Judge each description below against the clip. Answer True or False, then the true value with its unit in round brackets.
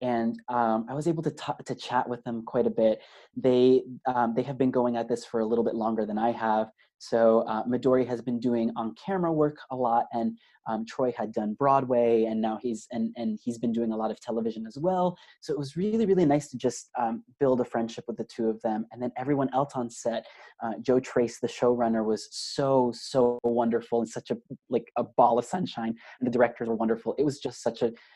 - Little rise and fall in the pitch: True (2.0 semitones)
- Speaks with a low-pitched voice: True (120 Hz)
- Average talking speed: False (235 wpm)